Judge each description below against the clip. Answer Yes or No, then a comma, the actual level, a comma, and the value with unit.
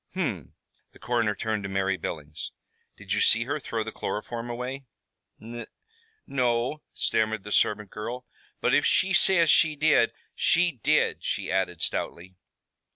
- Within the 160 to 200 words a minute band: No, average, 150 wpm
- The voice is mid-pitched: No, low, 115 Hz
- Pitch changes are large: No, average, 4.2 semitones